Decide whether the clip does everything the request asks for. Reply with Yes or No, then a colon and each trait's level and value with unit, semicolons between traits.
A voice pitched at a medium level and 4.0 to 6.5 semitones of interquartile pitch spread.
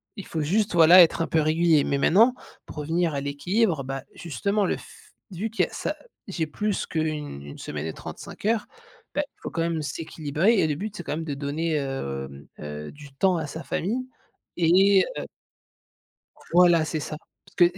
Yes: medium, 160 Hz; average, 4.5 semitones